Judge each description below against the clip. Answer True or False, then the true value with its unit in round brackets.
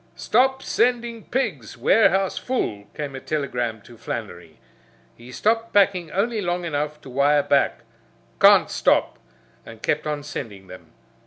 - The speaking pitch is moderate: True (150 Hz)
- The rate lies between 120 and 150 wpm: True (140 wpm)